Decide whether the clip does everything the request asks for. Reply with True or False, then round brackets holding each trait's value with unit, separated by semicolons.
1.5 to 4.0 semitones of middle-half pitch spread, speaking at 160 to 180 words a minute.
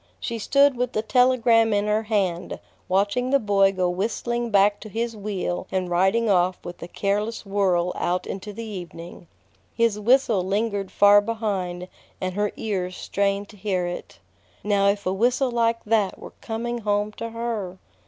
True (3.3 semitones; 170 wpm)